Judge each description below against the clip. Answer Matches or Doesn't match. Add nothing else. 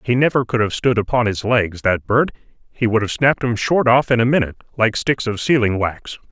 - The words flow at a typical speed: Doesn't match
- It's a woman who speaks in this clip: Doesn't match